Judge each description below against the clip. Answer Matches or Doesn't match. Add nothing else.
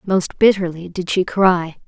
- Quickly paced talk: Doesn't match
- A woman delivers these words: Matches